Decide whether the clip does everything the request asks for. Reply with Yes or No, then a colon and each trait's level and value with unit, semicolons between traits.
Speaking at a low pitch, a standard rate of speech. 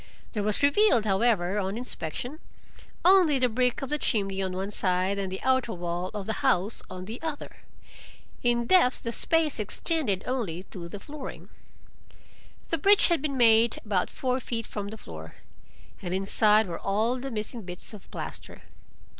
No: high, 220 Hz; average, 170 wpm